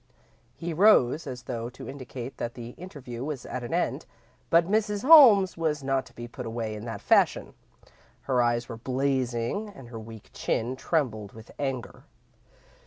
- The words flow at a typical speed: Yes, average, 170 wpm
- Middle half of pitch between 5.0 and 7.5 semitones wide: Yes, wide, 5.6 semitones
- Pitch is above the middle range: No, low, 130 Hz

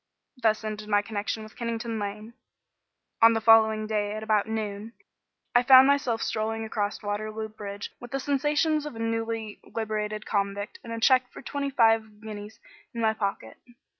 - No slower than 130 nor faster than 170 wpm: Yes, average, 165 wpm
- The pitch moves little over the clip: Yes, narrow, 1.4 semitones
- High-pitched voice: Yes, high, 220 Hz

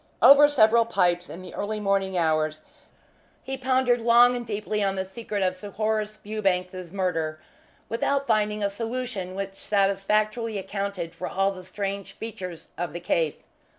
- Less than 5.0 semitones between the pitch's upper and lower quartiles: Yes, average, 3.2 semitones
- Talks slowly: No, average, 155 wpm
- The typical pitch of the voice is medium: No, high, 200 Hz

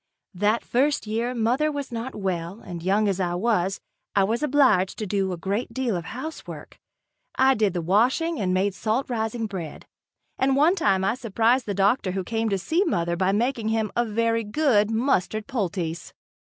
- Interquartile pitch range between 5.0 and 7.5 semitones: No, average, 4.4 semitones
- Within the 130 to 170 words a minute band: No, average, 185 wpm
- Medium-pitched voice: No, high, 215 Hz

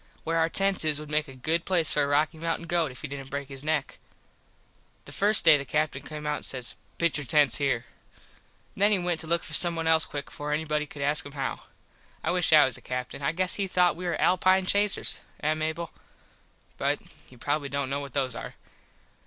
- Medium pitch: Yes, medium, 155 Hz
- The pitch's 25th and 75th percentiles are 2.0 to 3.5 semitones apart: Yes, average, 3.1 semitones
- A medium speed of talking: No, fast, 220 wpm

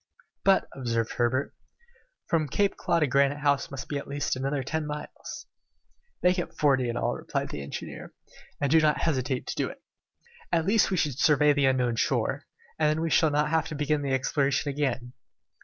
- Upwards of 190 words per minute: Yes, average, 200 wpm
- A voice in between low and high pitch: Yes, medium, 145 Hz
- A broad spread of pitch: No, average, 2.8 semitones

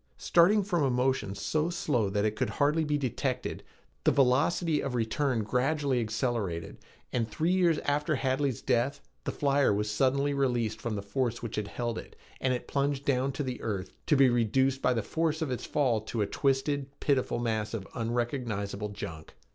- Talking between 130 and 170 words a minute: No, average, 180 wpm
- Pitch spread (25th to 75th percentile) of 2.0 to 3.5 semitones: No, average, 4.2 semitones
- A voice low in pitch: Yes, low, 130 Hz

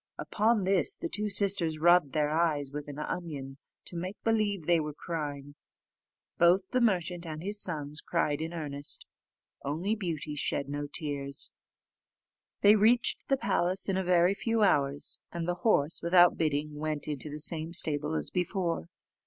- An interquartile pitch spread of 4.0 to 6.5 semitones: Yes, average, 4.3 semitones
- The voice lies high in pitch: No, medium, 165 Hz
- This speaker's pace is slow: No, average, 160 wpm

